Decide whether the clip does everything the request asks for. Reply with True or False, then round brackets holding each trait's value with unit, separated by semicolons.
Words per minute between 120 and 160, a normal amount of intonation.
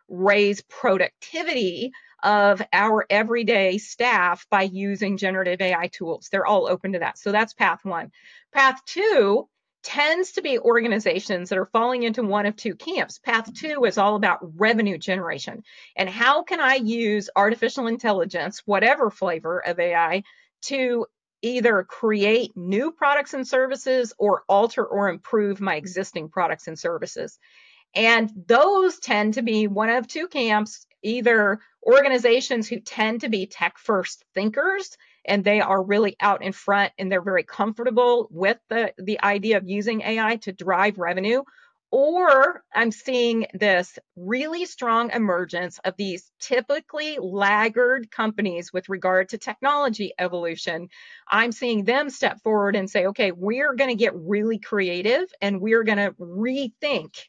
True (150 wpm; 4.2 semitones)